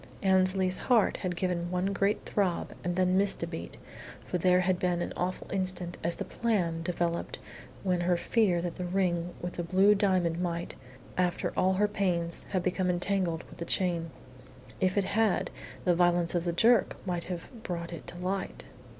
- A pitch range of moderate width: No, narrow, 1.6 semitones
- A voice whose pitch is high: No, medium, 180 Hz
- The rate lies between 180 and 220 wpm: Yes, average, 185 wpm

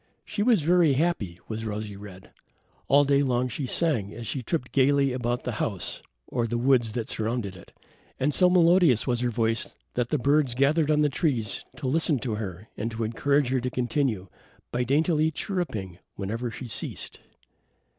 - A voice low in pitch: Yes, low, 125 Hz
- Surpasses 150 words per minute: Yes, average, 180 wpm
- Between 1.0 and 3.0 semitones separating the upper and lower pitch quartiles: No, average, 4.6 semitones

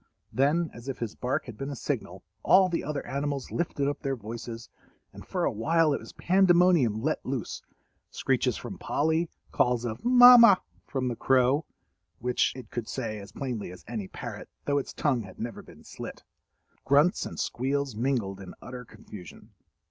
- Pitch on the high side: No, low, 135 Hz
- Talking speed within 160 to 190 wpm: Yes, average, 170 wpm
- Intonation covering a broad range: No, average, 4.5 semitones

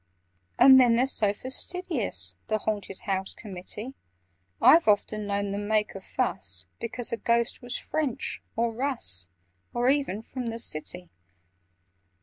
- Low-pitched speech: No, high, 225 Hz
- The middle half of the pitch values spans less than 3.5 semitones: No, average, 3.9 semitones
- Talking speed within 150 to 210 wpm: No, slow, 135 wpm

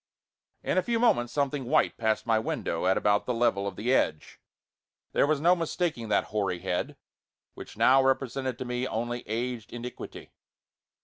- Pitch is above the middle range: No, low, 120 Hz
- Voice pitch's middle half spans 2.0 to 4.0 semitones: Yes, average, 3.5 semitones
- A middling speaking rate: Yes, average, 170 wpm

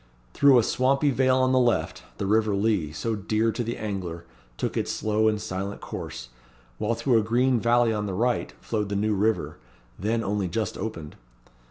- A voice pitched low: Yes, low, 110 Hz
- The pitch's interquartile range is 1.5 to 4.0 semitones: Yes, average, 2.9 semitones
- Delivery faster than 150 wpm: Yes, average, 190 wpm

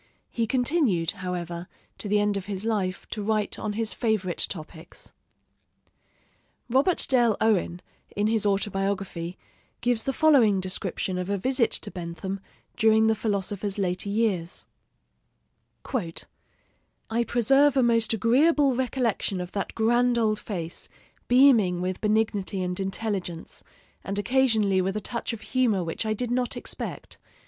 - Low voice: No, high, 210 Hz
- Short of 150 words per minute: Yes, average, 140 wpm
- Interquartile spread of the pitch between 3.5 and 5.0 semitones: Yes, average, 3.8 semitones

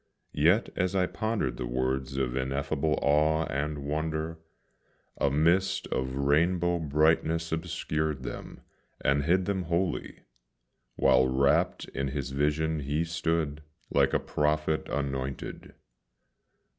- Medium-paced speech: No, slow, 120 wpm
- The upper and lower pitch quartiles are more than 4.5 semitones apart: No, average, 3.2 semitones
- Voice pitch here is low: Yes, very low, 75 Hz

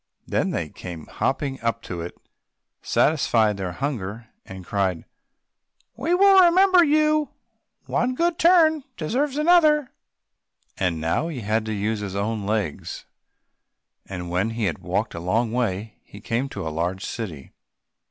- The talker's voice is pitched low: Yes, low, 115 Hz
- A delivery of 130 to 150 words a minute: Yes, average, 140 wpm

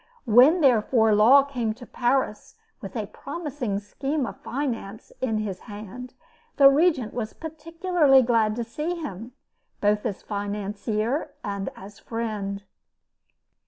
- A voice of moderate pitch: No, high, 235 Hz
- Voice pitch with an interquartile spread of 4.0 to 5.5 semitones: Yes, average, 4.7 semitones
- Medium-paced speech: No, slow, 125 wpm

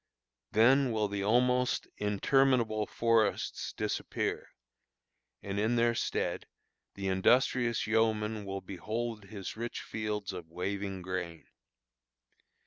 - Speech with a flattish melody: No, average, 3.1 semitones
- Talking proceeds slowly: Yes, slow, 105 wpm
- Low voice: Yes, low, 110 Hz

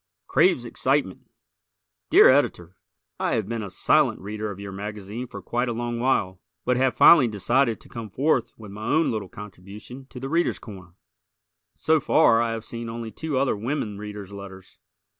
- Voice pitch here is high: No, low, 115 Hz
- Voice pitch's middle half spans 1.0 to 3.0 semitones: No, average, 4.1 semitones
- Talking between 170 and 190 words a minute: Yes, average, 180 wpm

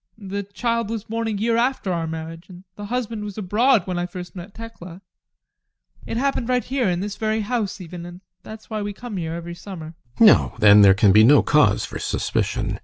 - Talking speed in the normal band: No, fast, 215 wpm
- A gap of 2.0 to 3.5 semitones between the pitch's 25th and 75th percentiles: No, average, 4.8 semitones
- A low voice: No, high, 200 Hz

